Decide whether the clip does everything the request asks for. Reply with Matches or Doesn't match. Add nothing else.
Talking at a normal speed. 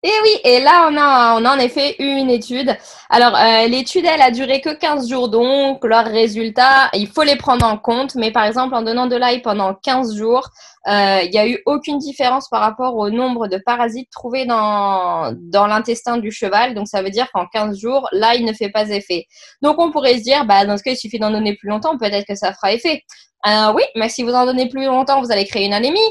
Doesn't match